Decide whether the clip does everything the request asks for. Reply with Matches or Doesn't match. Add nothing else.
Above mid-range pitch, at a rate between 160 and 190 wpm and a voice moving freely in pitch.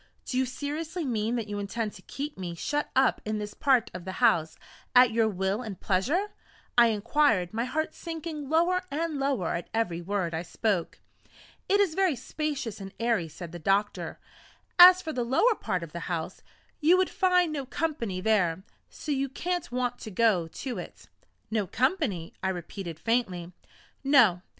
Matches